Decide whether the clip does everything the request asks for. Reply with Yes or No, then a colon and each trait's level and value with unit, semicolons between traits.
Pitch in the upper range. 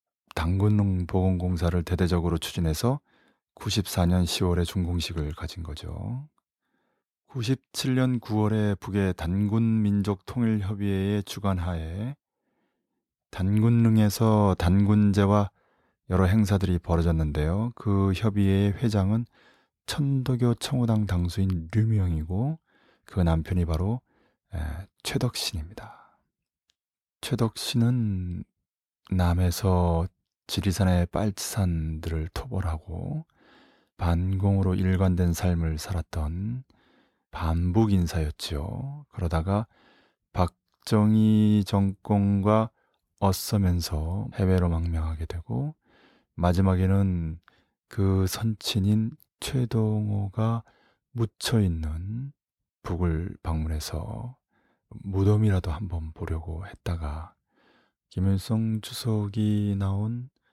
No: very low, 95 Hz